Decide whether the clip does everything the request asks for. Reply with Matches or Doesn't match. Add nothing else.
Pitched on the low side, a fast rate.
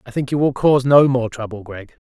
Matches